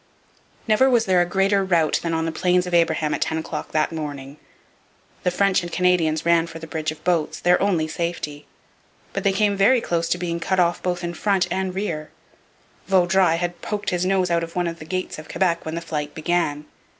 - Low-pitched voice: No, medium, 175 Hz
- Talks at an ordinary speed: No, fast, 215 wpm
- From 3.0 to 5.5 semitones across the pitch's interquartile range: No, narrow, 2.4 semitones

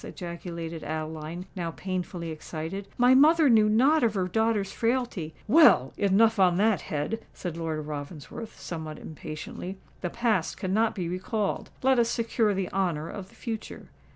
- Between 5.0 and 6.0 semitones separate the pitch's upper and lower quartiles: Yes, average, 5.3 semitones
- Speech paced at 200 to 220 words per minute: No, average, 150 wpm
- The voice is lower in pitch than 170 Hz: No, high, 190 Hz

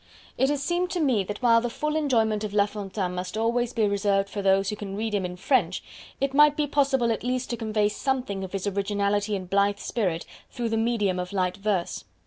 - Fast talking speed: Yes, fast, 225 wpm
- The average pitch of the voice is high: Yes, high, 210 Hz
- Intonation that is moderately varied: Yes, average, 3.7 semitones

